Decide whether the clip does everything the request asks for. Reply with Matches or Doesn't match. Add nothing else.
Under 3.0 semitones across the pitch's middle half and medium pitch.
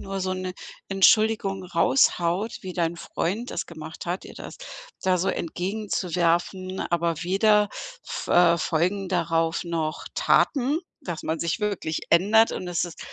Matches